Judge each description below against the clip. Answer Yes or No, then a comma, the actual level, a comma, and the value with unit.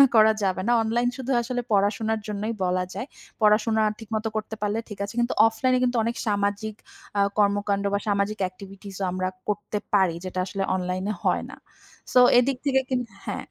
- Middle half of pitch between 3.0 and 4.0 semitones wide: No, narrow, 2.4 semitones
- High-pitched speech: Yes, high, 210 Hz